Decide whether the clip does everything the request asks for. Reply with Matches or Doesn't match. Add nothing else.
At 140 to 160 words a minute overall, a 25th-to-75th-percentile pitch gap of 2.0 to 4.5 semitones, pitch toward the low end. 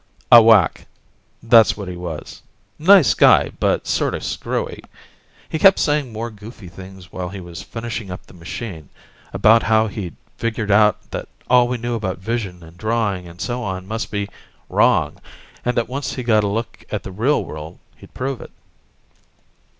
Doesn't match